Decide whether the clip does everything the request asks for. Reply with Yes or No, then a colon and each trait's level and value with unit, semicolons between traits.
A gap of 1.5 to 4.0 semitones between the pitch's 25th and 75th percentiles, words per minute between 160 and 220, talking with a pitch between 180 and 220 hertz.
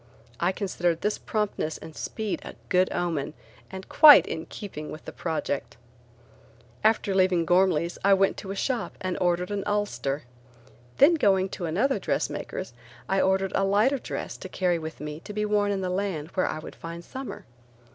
Yes: average, 3.4 semitones; average, 175 wpm; high, 190 Hz